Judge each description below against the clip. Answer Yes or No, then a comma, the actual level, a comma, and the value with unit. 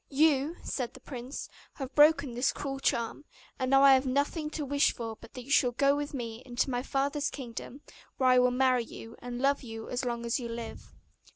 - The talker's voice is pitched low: No, very high, 260 Hz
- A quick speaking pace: Yes, fast, 215 wpm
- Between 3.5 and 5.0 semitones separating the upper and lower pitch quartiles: No, narrow, 2.5 semitones